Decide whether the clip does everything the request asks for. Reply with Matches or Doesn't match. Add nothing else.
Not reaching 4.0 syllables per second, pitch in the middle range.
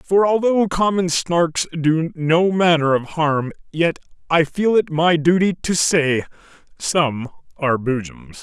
Matches